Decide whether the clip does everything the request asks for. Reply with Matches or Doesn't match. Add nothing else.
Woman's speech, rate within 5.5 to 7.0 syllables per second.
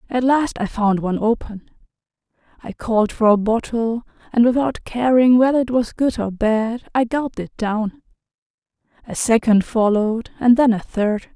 Doesn't match